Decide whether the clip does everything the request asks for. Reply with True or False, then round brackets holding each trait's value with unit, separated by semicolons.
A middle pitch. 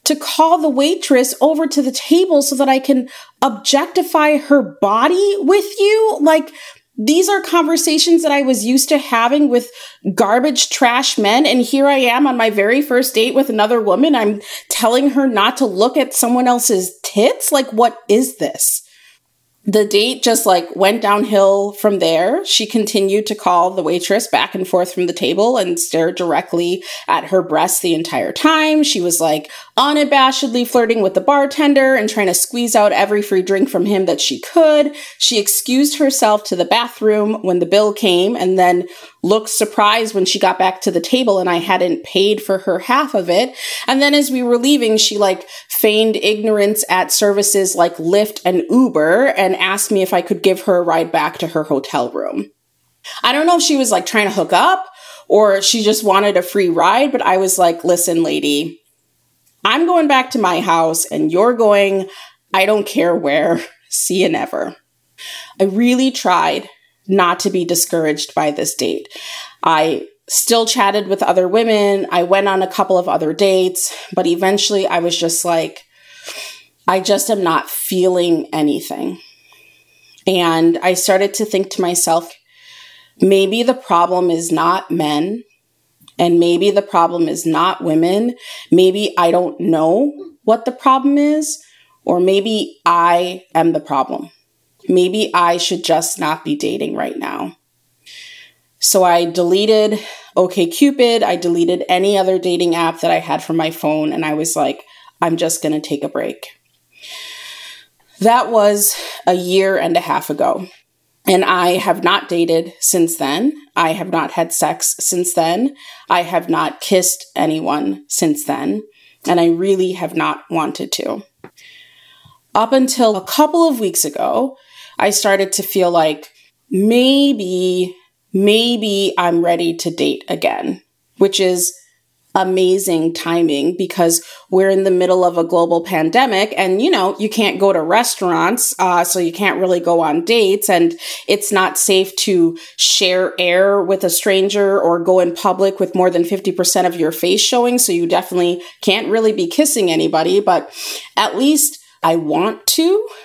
False (200 Hz)